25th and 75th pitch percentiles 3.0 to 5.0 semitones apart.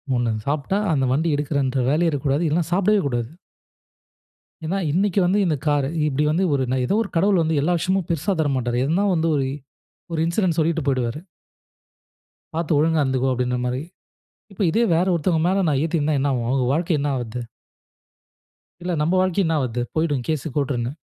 Yes: average, 4.3 semitones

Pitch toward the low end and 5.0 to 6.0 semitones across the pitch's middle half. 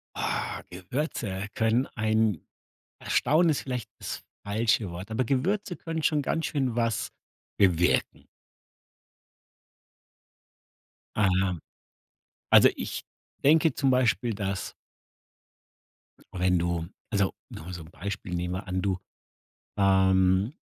Yes: low, 100 Hz; wide, 5.5 semitones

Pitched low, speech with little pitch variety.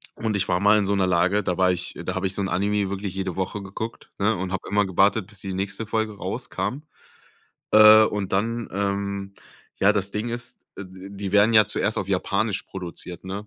Yes: low, 100 Hz; narrow, 1.9 semitones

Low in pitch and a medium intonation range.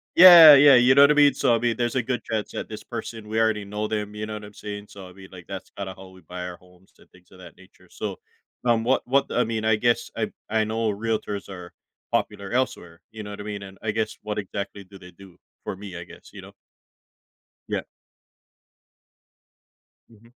Yes: low, 105 Hz; average, 3.2 semitones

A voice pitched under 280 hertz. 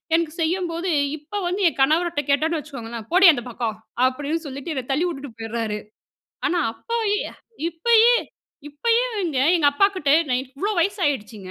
No: very high, 305 Hz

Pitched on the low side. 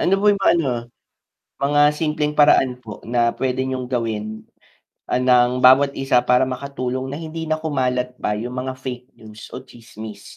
Yes: low, 130 Hz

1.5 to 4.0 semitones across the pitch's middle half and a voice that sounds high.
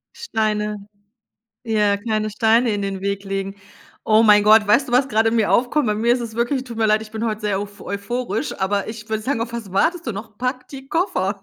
Yes: narrow, 2.5 semitones; high, 220 Hz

